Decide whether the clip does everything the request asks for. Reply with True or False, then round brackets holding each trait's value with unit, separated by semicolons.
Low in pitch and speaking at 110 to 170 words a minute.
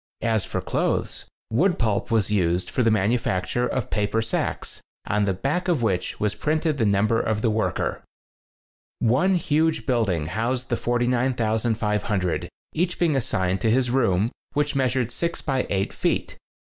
True (115 Hz; 160 wpm)